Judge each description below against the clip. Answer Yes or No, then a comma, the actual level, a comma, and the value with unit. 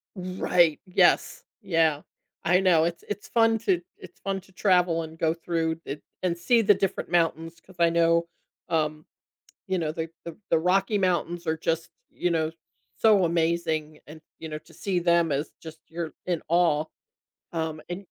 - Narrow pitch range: Yes, narrow, 2.1 semitones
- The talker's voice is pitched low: No, medium, 170 Hz